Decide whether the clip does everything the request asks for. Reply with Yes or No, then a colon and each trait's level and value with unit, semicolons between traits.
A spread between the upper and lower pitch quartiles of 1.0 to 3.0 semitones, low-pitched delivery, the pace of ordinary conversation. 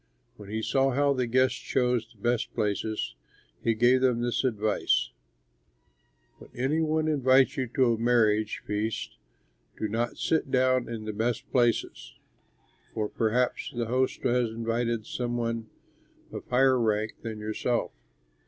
Yes: narrow, 2.6 semitones; low, 120 Hz; average, 145 wpm